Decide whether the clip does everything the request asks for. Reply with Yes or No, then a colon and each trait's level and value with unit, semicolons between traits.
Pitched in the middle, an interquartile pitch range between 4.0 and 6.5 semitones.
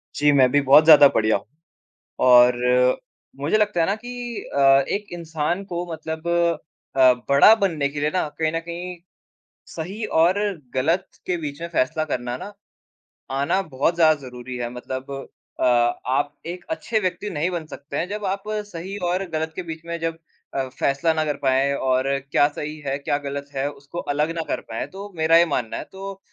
Yes: medium, 155 Hz; average, 4.3 semitones